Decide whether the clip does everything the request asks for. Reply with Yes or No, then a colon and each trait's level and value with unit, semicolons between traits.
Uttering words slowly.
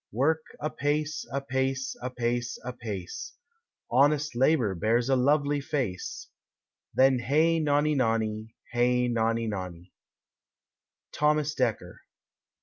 Yes: slow, 95 wpm